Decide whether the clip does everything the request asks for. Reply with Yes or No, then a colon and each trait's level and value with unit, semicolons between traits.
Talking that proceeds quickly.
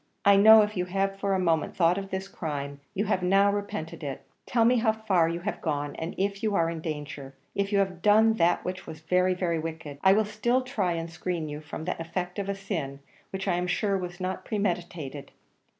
Yes: fast, 230 wpm